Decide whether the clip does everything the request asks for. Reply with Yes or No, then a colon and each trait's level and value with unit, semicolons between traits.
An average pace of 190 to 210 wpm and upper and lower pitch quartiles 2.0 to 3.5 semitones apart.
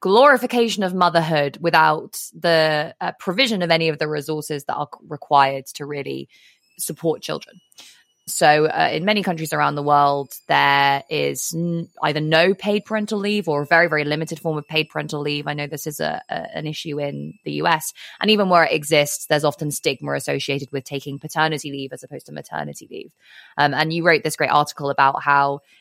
Yes: average, 195 wpm; average, 2.8 semitones